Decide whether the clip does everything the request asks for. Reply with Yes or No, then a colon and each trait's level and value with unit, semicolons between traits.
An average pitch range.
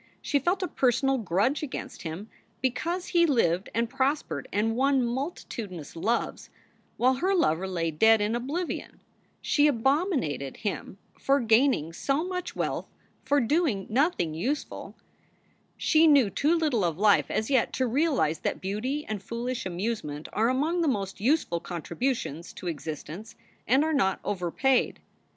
No: wide, 6.9 semitones